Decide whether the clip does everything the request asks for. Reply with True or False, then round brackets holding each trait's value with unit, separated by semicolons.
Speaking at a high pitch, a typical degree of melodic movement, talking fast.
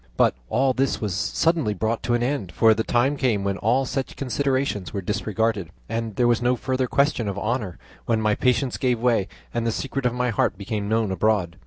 False (115 Hz; 3.5 semitones; 210 wpm)